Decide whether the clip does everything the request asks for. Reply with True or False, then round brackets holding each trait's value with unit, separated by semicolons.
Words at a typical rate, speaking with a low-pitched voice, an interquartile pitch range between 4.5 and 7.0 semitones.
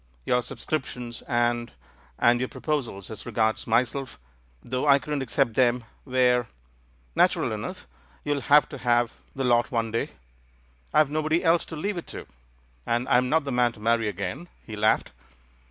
False (170 wpm; 120 Hz; 3.4 semitones)